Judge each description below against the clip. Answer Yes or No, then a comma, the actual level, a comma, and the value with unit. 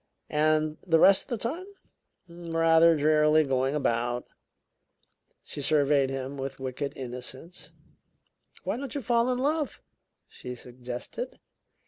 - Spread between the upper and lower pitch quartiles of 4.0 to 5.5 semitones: Yes, average, 4.8 semitones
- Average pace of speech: No, slow, 120 wpm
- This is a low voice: No, medium, 150 Hz